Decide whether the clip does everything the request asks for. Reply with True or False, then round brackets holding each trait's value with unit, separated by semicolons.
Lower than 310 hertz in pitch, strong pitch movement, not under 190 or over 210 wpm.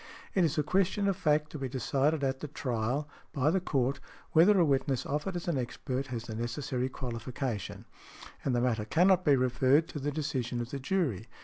False (135 Hz; 3.7 semitones; 200 wpm)